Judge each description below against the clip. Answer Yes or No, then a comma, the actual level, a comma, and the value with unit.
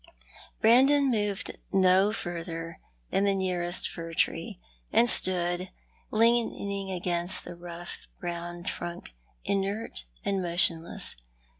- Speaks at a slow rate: Yes, slow, 110 wpm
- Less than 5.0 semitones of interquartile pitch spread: Yes, narrow, 2.6 semitones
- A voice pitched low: No, medium, 185 Hz